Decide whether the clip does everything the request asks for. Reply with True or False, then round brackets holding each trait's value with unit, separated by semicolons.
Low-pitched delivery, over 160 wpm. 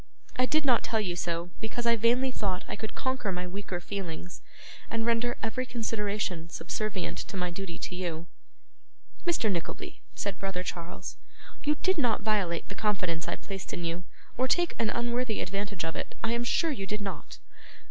False (205 Hz; 180 wpm)